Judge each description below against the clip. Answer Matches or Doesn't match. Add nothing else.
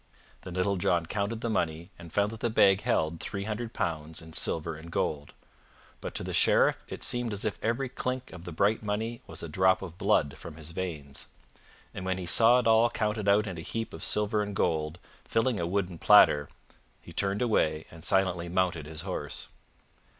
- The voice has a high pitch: Doesn't match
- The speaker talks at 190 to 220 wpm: Matches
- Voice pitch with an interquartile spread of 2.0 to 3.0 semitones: Doesn't match